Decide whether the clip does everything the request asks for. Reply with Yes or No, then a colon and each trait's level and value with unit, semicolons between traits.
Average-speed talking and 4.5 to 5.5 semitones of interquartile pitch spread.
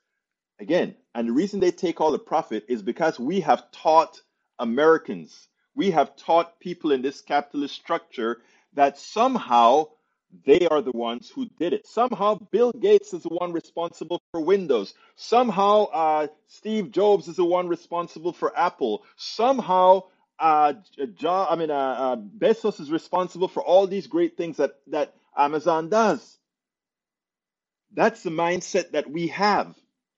Yes: average, 155 wpm; average, 5.1 semitones